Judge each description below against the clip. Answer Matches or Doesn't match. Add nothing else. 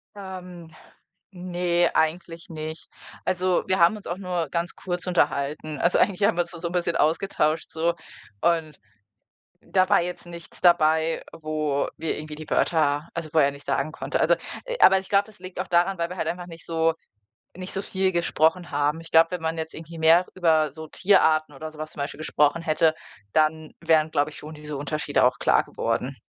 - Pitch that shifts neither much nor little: Doesn't match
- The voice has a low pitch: Doesn't match